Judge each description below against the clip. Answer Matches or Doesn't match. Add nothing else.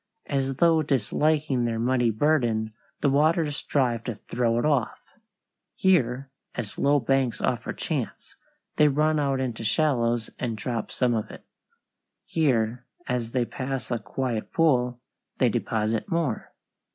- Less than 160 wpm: Matches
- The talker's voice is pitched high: Doesn't match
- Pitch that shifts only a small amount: Doesn't match